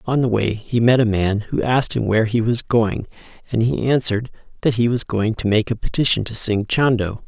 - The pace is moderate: No, fast, 230 wpm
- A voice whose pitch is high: No, low, 115 Hz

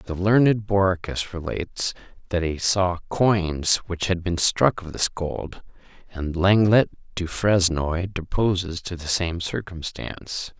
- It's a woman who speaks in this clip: No, male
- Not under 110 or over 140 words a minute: Yes, slow, 135 wpm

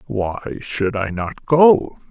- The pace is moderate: Yes, average, 145 wpm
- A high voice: No, low, 120 Hz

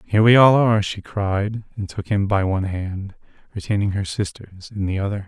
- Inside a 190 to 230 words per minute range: Yes, fast, 205 wpm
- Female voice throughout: No, male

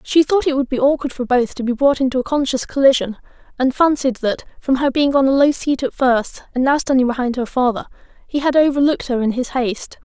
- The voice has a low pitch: No, very high, 265 Hz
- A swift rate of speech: Yes, fast, 230 wpm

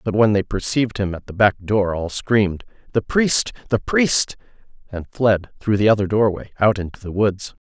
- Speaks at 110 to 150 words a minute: No, average, 190 wpm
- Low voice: Yes, low, 105 Hz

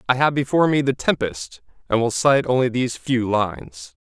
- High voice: No, low, 120 Hz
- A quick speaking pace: No, average, 195 wpm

